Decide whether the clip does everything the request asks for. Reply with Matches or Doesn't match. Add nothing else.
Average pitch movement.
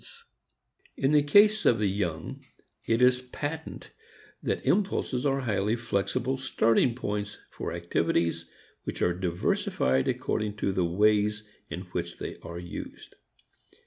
Doesn't match